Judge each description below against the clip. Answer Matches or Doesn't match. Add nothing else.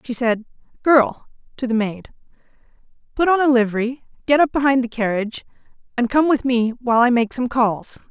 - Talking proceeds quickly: Doesn't match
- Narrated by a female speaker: Matches